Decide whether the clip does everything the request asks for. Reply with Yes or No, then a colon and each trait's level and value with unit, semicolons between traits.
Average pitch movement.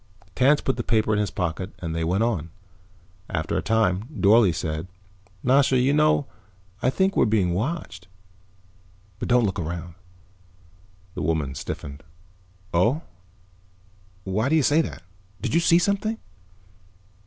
No: wide, 7.9 semitones